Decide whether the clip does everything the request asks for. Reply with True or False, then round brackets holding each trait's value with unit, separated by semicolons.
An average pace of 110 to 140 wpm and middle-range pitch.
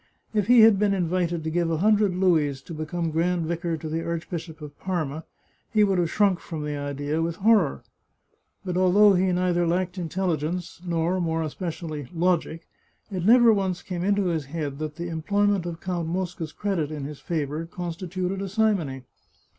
False (180 wpm; 175 Hz)